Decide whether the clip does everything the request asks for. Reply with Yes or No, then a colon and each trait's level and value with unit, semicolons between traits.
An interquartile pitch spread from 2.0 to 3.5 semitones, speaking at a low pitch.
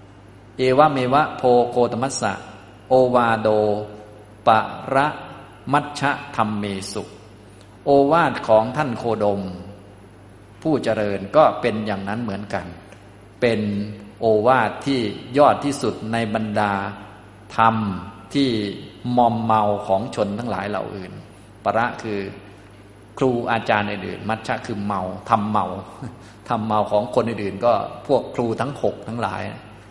Yes: average, 2.9 semitones; low, 105 Hz